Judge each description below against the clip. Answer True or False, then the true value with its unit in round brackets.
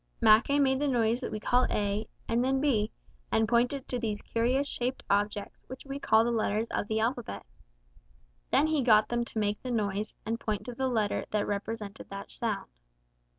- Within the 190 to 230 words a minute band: True (195 wpm)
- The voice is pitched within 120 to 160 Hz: False (230 Hz)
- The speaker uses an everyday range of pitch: True (3.2 semitones)